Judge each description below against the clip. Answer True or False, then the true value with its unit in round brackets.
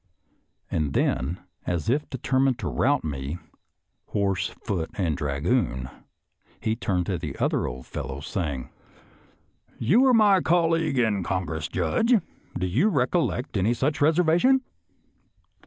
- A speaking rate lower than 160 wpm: True (140 wpm)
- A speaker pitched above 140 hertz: False (105 Hz)